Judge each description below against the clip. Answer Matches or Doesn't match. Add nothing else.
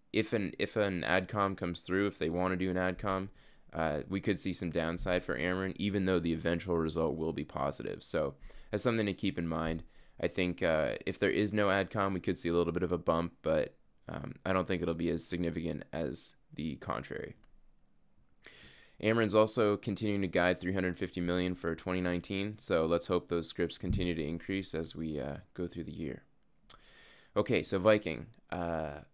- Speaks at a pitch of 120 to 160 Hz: Doesn't match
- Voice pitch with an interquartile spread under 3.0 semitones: Matches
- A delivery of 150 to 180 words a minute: Doesn't match